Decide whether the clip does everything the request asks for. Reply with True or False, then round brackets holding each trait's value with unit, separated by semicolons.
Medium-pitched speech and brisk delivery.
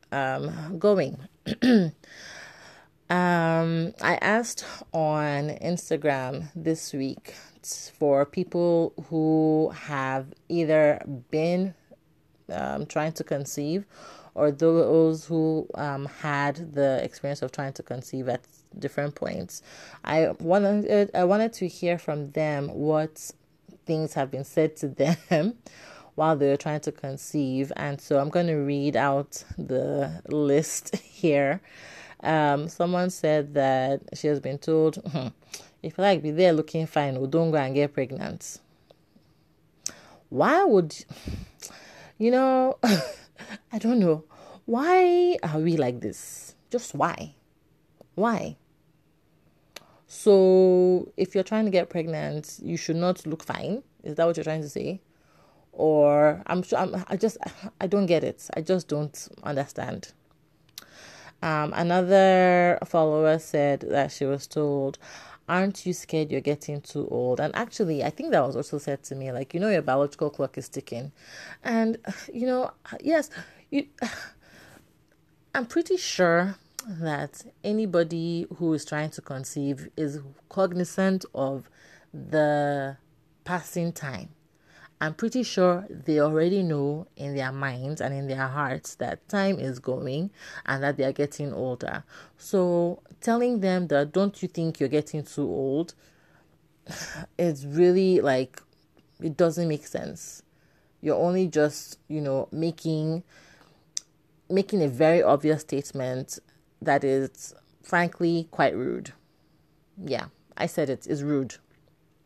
False (155 Hz; 135 wpm)